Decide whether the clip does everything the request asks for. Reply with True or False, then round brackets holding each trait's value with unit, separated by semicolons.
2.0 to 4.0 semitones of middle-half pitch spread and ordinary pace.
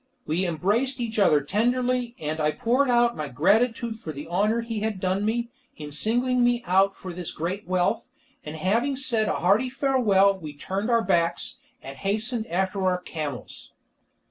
False (5.5 semitones; 170 wpm)